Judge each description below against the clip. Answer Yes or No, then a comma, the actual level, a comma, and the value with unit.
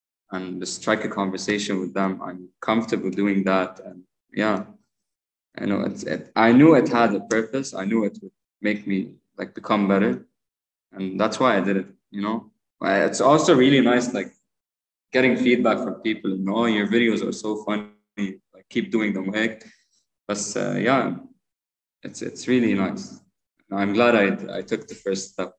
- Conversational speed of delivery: Yes, average, 190 wpm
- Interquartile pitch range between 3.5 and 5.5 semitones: No, average, 2.9 semitones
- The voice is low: Yes, low, 105 Hz